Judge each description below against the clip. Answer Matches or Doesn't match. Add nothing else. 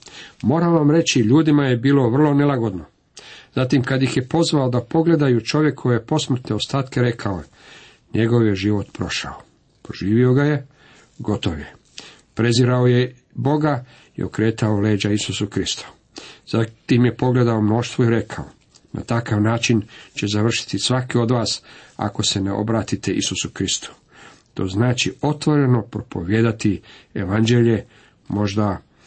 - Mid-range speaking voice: Doesn't match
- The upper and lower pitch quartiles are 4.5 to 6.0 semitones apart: Doesn't match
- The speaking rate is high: Doesn't match